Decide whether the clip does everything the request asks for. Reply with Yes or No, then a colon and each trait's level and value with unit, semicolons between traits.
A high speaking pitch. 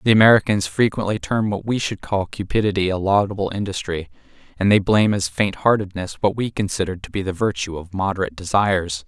No: low, 100 Hz